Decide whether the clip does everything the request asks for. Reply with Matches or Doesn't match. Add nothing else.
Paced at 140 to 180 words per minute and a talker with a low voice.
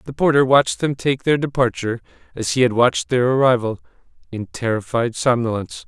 Matches